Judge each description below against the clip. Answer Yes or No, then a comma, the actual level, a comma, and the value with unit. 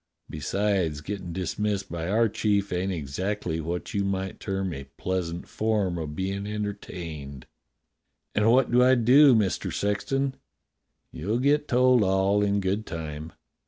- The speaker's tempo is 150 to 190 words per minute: No, average, 140 wpm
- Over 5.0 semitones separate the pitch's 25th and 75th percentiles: No, average, 3.6 semitones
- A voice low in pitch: Yes, low, 100 Hz